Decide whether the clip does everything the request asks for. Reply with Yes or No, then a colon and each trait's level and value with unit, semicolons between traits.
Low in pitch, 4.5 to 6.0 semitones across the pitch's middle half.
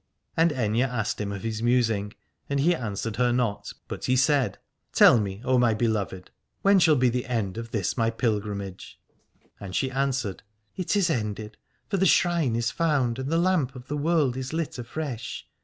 Yes: low, 125 Hz; average, 4.8 semitones